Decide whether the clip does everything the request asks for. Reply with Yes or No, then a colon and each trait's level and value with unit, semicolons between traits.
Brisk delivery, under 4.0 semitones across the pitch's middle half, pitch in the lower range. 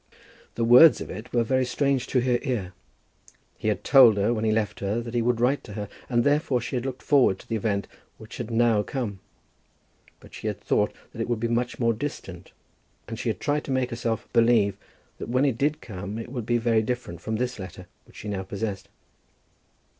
Yes: fast, 220 wpm; average, 2.8 semitones; low, 115 Hz